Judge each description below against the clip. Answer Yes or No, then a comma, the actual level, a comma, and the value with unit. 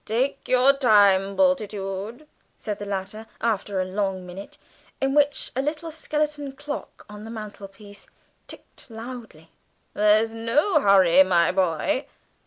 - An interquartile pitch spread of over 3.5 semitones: Yes, wide, 5.6 semitones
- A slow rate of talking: Yes, slow, 130 wpm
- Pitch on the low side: No, high, 215 Hz